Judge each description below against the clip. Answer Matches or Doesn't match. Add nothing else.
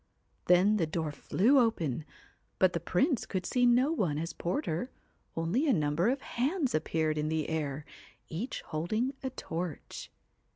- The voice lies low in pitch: Doesn't match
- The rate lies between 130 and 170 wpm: Matches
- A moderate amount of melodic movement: Doesn't match